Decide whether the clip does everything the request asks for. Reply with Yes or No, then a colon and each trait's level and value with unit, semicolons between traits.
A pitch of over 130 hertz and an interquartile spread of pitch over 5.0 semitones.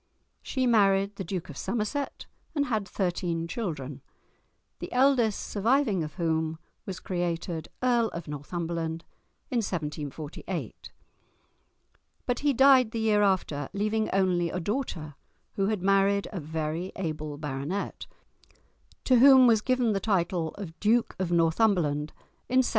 Yes: high, 190 Hz; wide, 5.4 semitones